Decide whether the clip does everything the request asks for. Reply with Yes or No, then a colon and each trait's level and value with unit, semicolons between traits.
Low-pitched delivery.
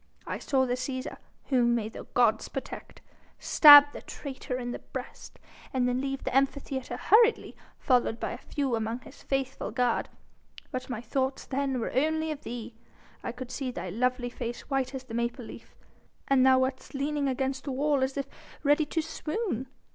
No: very high, 260 Hz